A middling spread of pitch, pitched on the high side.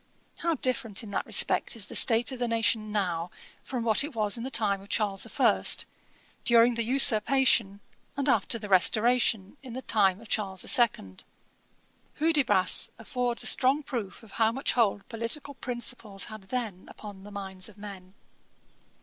Yes: average, 3.6 semitones; high, 225 Hz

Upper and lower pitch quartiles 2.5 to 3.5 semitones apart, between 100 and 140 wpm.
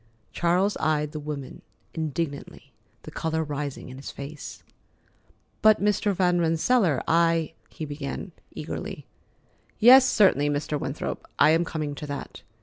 Yes: average, 3.2 semitones; slow, 135 wpm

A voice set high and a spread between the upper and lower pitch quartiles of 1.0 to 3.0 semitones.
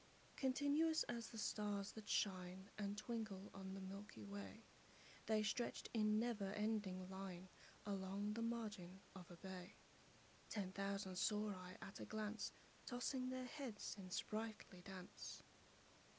Yes: high, 205 Hz; average, 2.7 semitones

